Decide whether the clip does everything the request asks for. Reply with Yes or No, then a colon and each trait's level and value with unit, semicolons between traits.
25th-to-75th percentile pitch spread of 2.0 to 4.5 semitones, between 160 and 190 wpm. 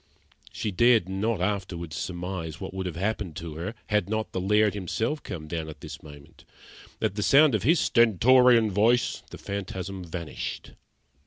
Yes: average, 4.0 semitones; average, 165 wpm